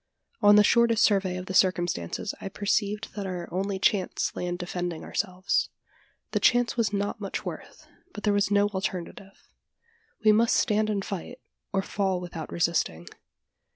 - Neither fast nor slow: Yes, average, 160 wpm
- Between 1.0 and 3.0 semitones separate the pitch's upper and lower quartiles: Yes, narrow, 2.5 semitones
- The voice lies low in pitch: No, high, 195 Hz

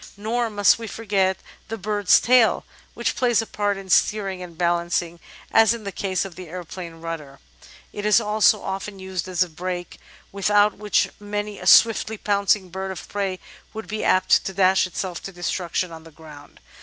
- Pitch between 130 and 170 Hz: No, high, 195 Hz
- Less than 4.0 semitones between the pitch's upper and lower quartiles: Yes, average, 2.7 semitones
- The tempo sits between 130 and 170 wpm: No, average, 180 wpm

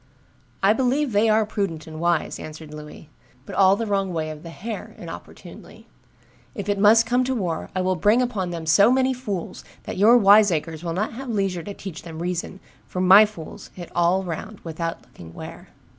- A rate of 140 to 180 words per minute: No, average, 195 wpm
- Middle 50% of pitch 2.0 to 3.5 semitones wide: No, average, 4.4 semitones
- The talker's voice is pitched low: No, high, 190 Hz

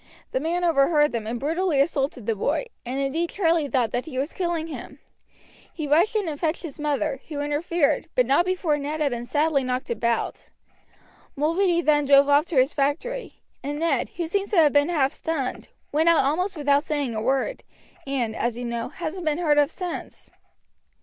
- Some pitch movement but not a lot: Yes, average, 3.6 semitones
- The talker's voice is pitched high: Yes, very high, 295 Hz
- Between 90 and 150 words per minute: No, average, 195 wpm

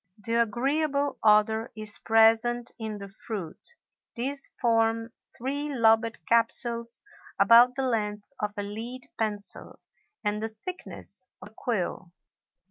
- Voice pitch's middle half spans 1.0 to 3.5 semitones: Yes, narrow, 2.4 semitones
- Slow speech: Yes, slow, 125 wpm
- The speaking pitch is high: Yes, high, 225 Hz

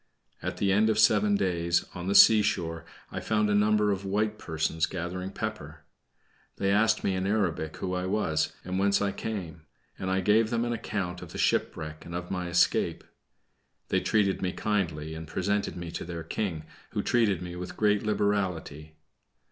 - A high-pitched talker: No, very low, 95 Hz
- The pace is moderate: Yes, average, 180 wpm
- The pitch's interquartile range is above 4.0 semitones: No, average, 3.3 semitones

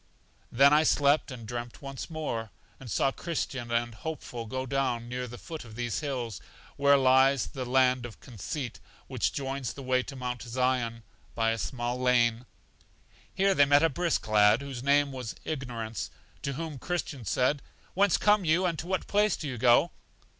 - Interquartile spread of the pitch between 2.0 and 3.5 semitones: Yes, average, 3.2 semitones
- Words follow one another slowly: No, average, 180 wpm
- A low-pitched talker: Yes, low, 130 Hz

